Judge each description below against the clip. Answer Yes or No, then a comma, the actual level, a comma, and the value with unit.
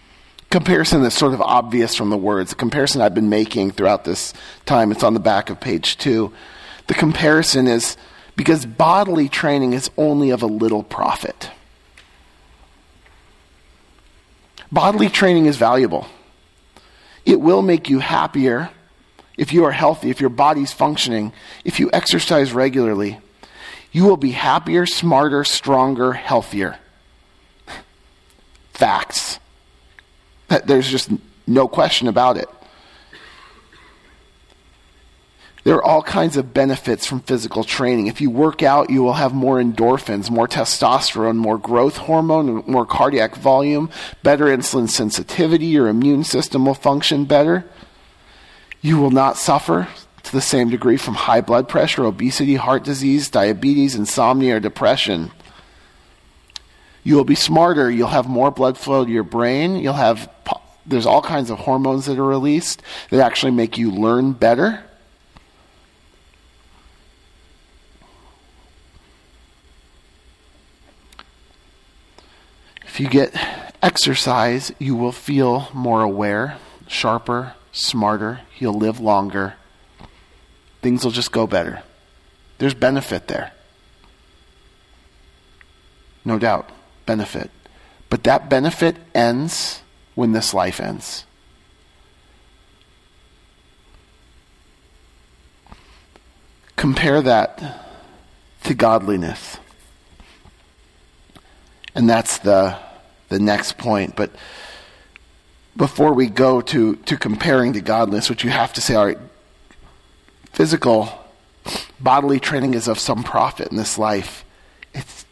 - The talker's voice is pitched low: Yes, low, 115 Hz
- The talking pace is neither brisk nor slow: No, slow, 115 wpm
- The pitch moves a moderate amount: No, wide, 8.5 semitones